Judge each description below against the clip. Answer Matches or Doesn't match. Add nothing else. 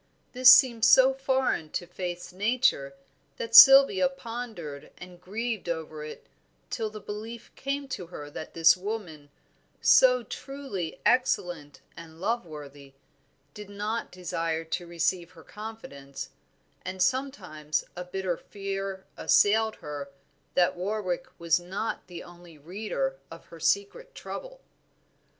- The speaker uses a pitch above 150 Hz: Matches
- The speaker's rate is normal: Doesn't match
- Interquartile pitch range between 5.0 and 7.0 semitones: Matches